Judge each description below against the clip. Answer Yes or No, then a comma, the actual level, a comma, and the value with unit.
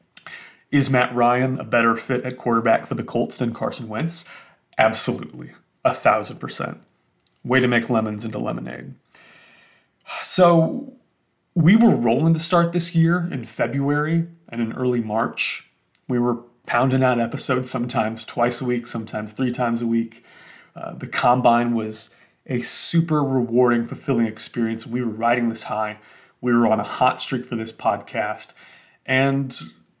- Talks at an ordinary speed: Yes, average, 150 wpm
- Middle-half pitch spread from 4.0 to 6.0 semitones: No, average, 2.7 semitones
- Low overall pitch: Yes, low, 120 Hz